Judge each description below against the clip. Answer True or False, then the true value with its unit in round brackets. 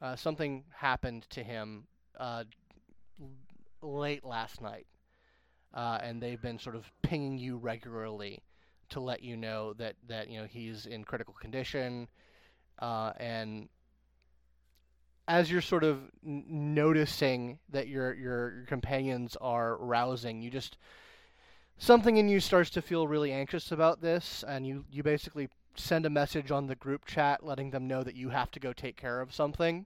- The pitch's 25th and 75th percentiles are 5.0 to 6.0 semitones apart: False (4.4 semitones)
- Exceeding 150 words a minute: True (160 wpm)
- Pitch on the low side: True (130 Hz)